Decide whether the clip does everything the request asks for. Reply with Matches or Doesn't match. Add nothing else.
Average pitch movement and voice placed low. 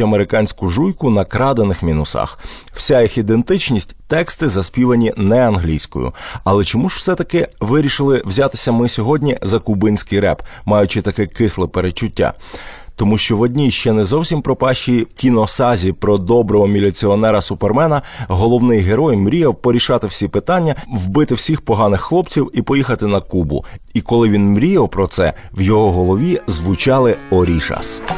Matches